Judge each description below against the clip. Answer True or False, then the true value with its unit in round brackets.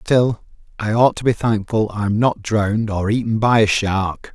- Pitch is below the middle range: True (110 Hz)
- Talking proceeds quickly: False (195 wpm)